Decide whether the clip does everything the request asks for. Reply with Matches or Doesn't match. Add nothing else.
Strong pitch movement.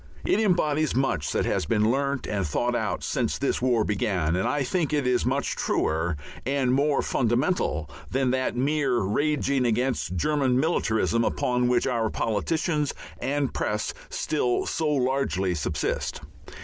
Doesn't match